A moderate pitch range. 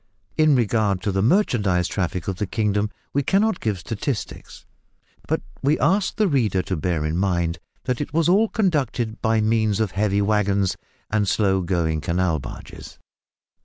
No: wide, 5.7 semitones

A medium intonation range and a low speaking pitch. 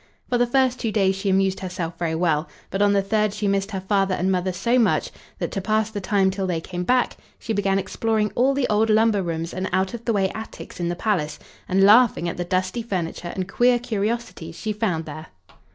No: average, 3.3 semitones; high, 195 Hz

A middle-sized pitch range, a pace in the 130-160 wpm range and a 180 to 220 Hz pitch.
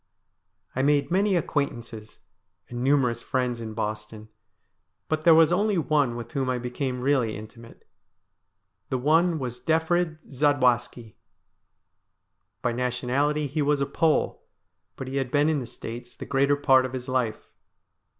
No: average, 3.5 semitones; average, 145 wpm; low, 130 Hz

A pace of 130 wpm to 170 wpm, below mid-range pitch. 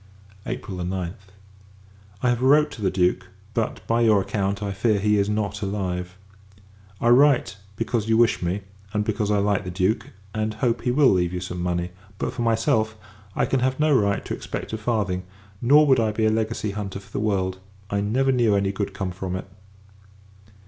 No: average, 195 wpm; low, 105 Hz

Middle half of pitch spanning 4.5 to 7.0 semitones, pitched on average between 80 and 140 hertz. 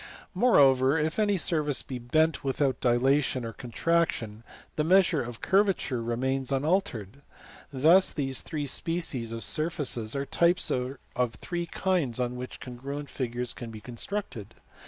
Yes: average, 5.0 semitones; low, 135 Hz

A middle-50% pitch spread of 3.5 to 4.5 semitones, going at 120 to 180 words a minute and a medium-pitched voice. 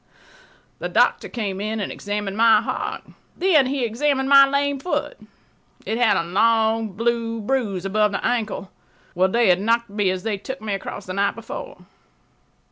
No: average, 3.8 semitones; average, 165 wpm; high, 225 Hz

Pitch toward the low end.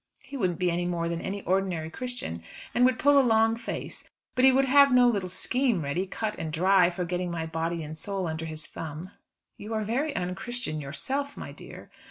No: medium, 185 Hz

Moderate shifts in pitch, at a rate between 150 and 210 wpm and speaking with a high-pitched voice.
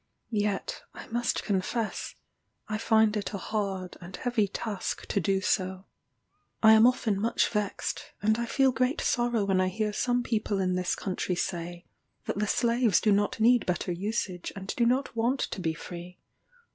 Yes: average, 3.8 semitones; average, 175 wpm; high, 210 Hz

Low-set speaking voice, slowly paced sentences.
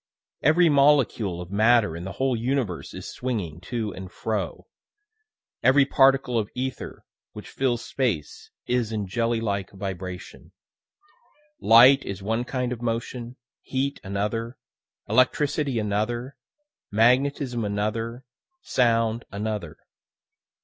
Yes: low, 115 Hz; slow, 115 wpm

